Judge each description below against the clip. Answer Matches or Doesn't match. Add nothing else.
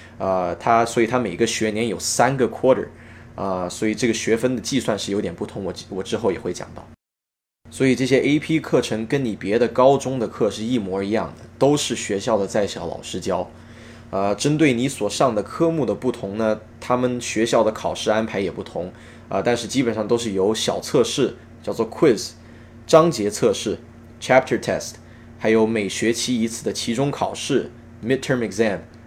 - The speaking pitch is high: Doesn't match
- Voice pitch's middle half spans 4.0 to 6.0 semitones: Doesn't match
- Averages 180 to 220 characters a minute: Doesn't match